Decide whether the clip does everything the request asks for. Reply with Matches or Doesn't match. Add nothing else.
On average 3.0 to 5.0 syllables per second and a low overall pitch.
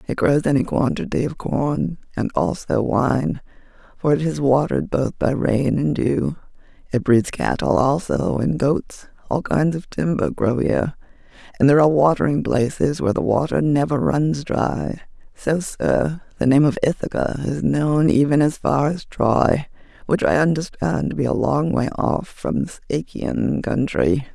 Doesn't match